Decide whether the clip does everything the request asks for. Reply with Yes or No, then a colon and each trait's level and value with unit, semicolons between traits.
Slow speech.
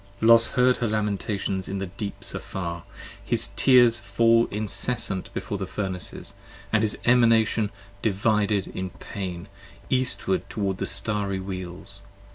Yes: slow, 130 wpm